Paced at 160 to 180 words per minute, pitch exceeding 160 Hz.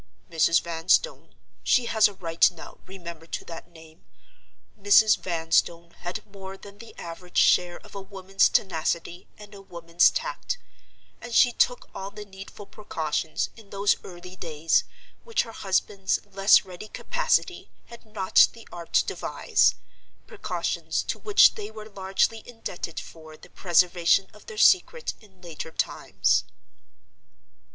No: slow, 135 wpm; high, 190 Hz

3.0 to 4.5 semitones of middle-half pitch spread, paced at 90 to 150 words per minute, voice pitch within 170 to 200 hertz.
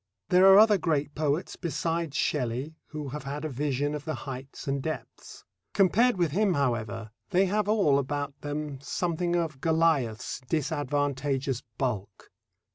No: average, 3.5 semitones; average, 145 wpm; medium, 145 Hz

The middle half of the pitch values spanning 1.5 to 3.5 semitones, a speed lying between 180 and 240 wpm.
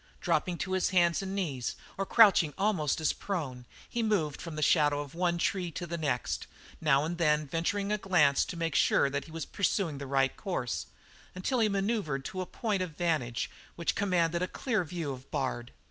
No: average, 4.5 semitones; average, 195 wpm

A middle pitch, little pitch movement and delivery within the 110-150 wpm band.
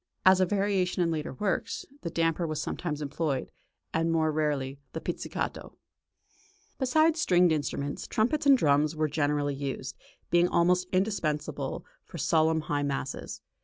No: medium, 160 Hz; average, 3.6 semitones; average, 140 wpm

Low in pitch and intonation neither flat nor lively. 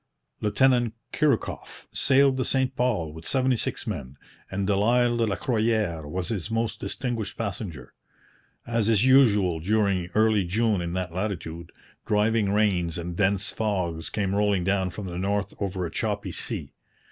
Yes: low, 105 Hz; average, 4.1 semitones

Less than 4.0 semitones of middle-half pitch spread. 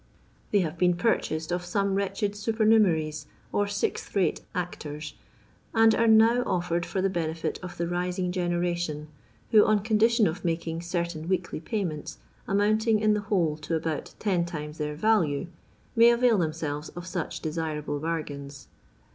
No: average, 4.5 semitones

